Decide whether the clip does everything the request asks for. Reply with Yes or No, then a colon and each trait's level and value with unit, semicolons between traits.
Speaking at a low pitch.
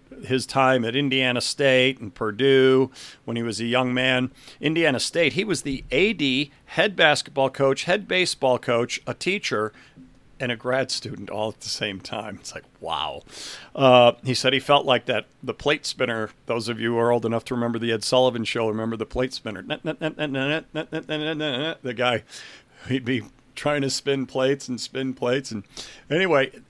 Yes: low, 130 Hz